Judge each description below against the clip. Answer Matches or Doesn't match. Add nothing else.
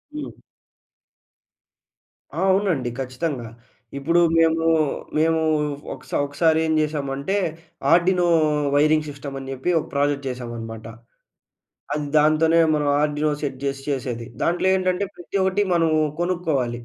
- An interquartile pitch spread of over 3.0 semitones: Matches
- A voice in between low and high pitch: Matches